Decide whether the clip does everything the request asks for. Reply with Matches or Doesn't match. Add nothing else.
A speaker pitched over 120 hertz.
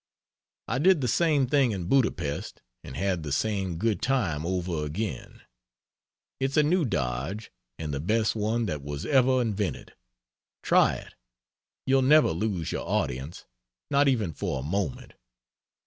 Doesn't match